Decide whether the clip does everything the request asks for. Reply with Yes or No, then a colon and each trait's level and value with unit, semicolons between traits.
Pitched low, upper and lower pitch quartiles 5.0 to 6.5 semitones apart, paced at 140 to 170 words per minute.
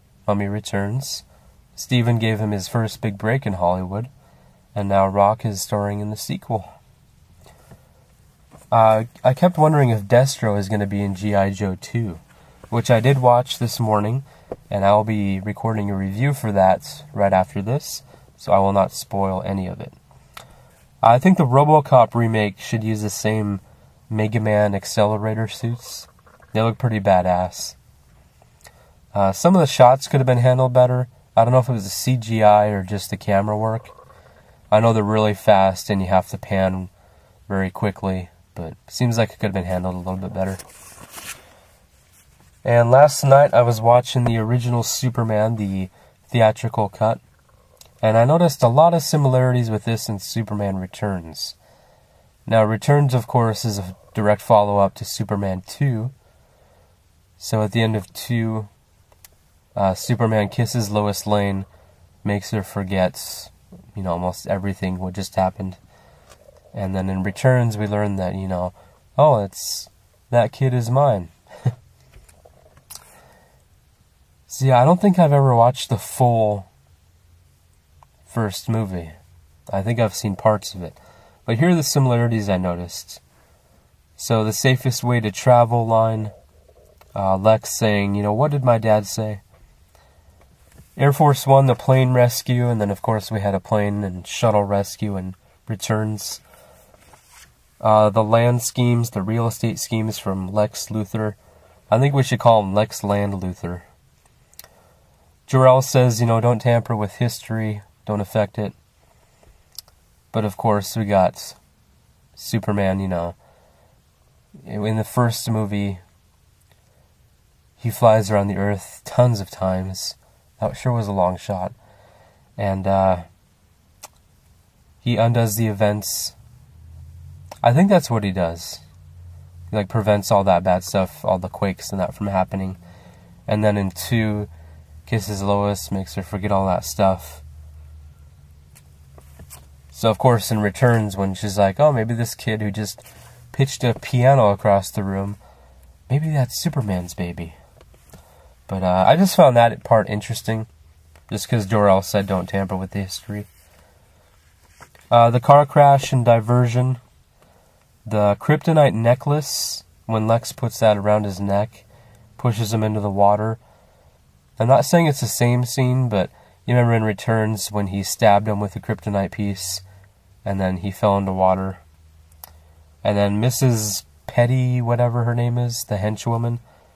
No: low, 105 Hz; average, 3.9 semitones; average, 150 wpm